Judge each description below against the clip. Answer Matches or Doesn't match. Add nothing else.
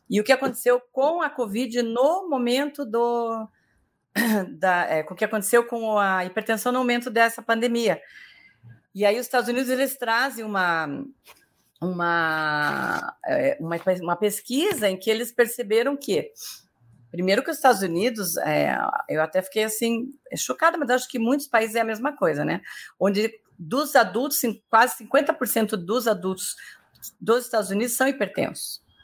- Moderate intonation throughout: Matches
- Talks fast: Doesn't match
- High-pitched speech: Matches